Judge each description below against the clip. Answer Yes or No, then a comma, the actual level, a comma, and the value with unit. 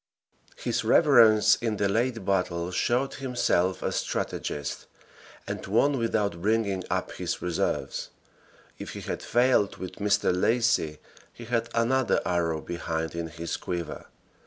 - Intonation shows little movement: No, average, 5.3 semitones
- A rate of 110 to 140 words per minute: Yes, slow, 135 wpm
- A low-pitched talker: Yes, low, 105 Hz